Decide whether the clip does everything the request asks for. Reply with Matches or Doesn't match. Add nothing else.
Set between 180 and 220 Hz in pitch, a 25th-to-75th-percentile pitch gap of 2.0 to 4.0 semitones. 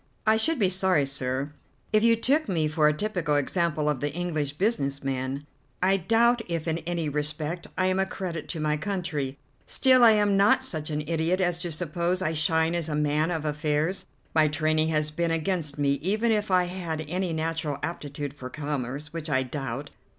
Doesn't match